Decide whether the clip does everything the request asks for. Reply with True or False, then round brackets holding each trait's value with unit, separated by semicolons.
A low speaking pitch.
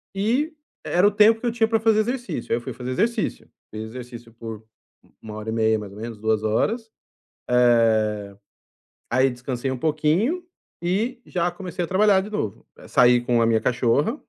True (130 Hz)